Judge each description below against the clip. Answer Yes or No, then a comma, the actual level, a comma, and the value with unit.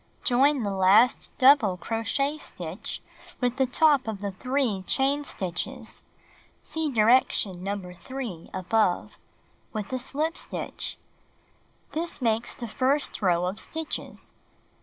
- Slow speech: Yes, slow, 120 wpm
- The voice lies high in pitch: Yes, high, 235 Hz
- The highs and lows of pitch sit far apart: Yes, wide, 5.9 semitones